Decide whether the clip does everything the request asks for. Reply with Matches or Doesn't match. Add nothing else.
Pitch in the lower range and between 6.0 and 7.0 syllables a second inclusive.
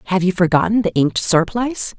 Doesn't match